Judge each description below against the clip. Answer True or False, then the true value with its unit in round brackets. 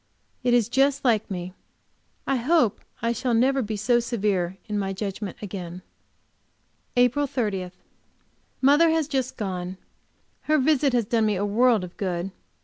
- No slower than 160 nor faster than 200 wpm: False (150 wpm)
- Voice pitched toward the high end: True (230 Hz)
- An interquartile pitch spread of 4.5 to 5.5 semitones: True (5.1 semitones)